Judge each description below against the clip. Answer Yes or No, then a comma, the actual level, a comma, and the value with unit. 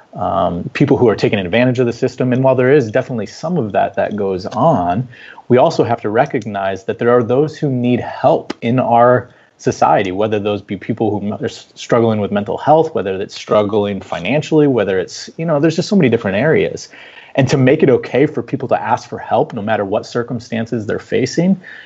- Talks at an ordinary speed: No, fast, 210 wpm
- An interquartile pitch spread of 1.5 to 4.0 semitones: No, average, 4.4 semitones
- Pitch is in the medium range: No, low, 120 Hz